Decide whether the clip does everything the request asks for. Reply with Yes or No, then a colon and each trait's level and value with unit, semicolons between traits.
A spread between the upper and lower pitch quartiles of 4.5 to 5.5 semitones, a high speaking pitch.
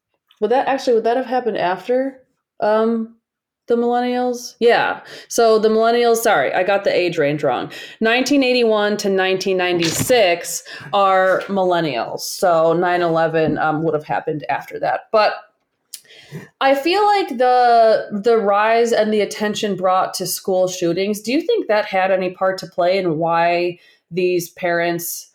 Yes: average, 5.0 semitones; high, 200 Hz